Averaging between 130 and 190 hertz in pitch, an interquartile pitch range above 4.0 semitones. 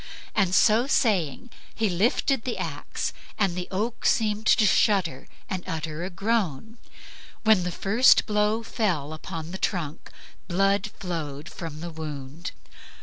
Yes: medium, 185 Hz; average, 4.9 semitones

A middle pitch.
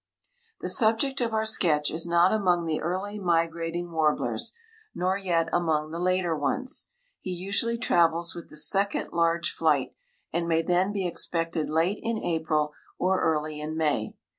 Yes: medium, 170 Hz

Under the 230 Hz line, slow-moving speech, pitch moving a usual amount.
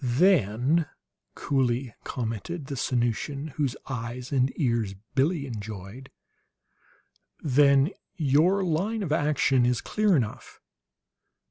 Yes: low, 135 Hz; slow, 100 wpm; average, 4.2 semitones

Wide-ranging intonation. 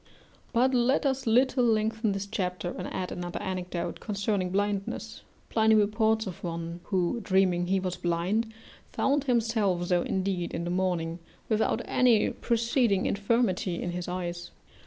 No: average, 4.0 semitones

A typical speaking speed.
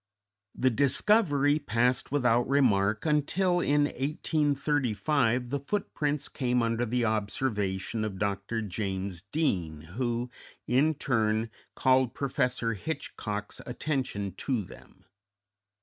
No: slow, 100 wpm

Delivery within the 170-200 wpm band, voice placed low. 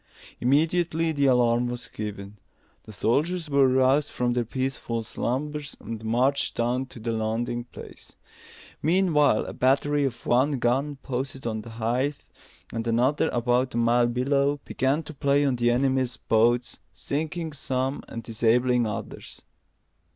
No: average, 145 wpm; low, 125 Hz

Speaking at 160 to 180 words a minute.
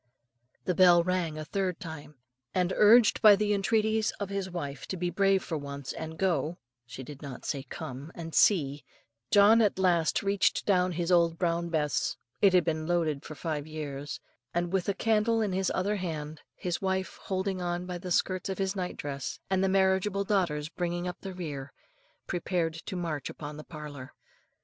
No: average, 190 wpm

